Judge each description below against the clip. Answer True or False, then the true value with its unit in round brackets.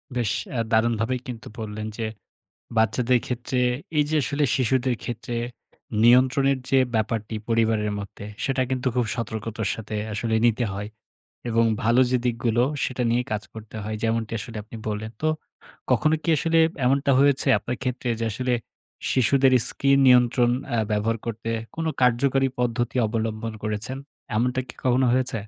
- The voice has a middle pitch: False (120 Hz)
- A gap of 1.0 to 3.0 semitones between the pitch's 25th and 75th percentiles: True (2.6 semitones)